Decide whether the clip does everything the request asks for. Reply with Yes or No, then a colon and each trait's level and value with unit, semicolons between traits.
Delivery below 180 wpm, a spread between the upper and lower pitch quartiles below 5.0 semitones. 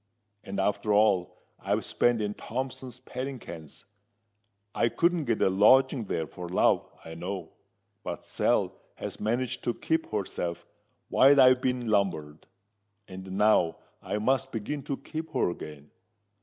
No: average, 140 wpm; wide, 5.6 semitones